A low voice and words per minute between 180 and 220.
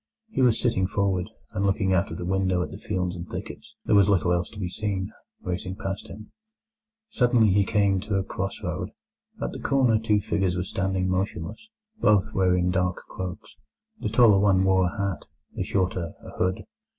Yes: very low, 95 Hz; average, 185 wpm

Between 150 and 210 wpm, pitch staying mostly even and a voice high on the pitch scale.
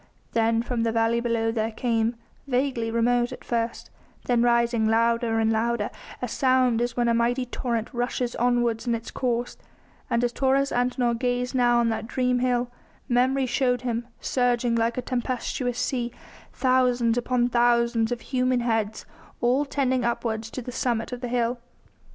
Yes: average, 165 wpm; narrow, 1.2 semitones; high, 240 Hz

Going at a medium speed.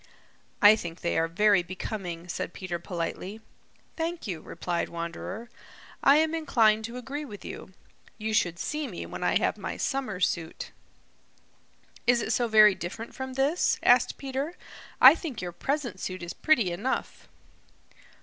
Yes: average, 155 wpm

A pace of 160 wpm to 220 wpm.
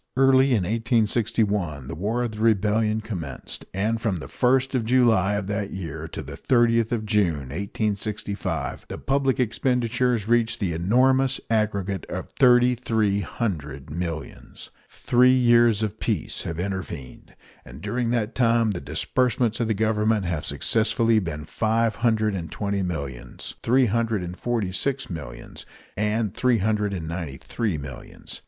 No: average, 150 wpm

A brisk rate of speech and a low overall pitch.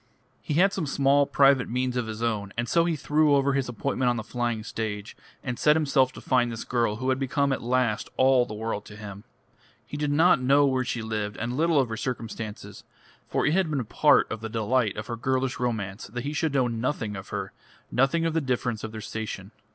Yes: fast, 230 wpm; low, 125 Hz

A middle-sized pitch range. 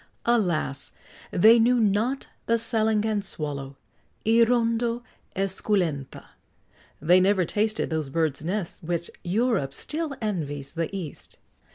No: wide, 6.0 semitones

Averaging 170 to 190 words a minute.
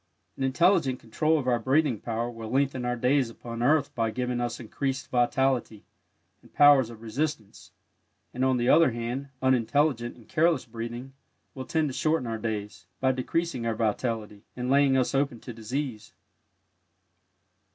No: average, 160 wpm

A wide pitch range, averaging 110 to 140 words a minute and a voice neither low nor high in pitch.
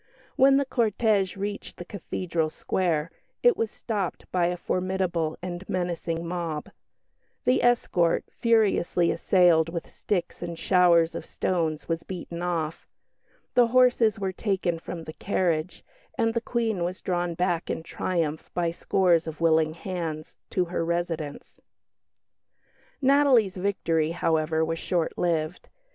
No: average, 2.9 semitones; slow, 135 wpm; medium, 175 Hz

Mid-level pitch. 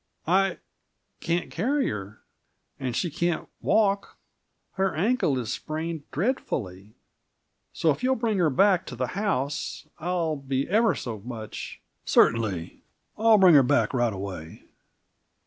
Yes: medium, 155 Hz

